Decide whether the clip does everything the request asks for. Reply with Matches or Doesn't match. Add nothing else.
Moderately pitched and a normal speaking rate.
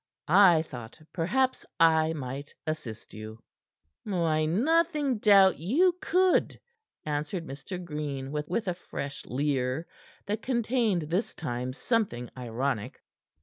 Doesn't match